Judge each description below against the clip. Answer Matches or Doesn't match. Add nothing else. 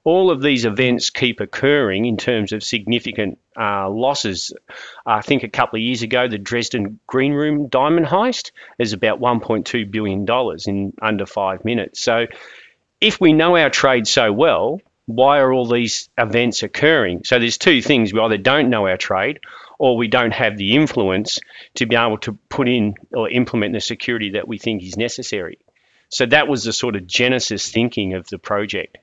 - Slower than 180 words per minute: Doesn't match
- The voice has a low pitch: Matches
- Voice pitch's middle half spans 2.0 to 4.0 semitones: Matches